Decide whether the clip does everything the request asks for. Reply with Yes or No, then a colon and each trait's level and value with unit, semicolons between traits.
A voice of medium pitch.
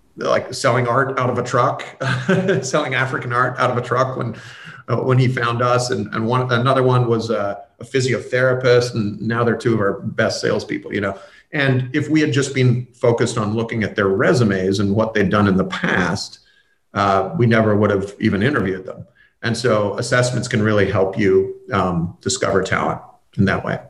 No: low, 120 Hz